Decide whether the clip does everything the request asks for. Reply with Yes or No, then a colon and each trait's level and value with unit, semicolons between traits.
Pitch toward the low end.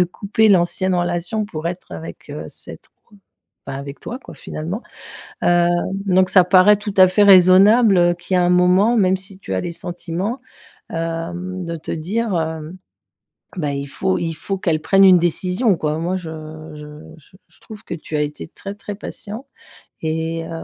No: medium, 180 Hz